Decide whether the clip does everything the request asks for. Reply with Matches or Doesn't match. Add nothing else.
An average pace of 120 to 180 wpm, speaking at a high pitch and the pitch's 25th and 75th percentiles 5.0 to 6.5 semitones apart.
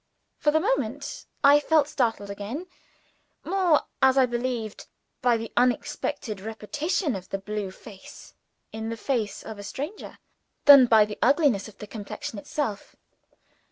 Matches